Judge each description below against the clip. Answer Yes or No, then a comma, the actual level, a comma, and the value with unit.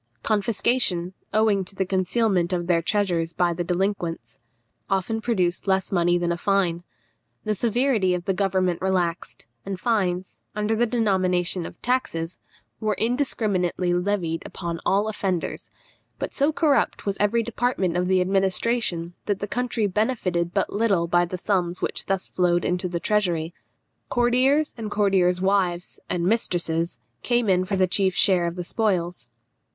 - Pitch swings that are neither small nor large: Yes, average, 3.3 semitones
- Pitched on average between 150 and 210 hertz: Yes, high, 190 Hz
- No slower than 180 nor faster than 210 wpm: No, average, 155 wpm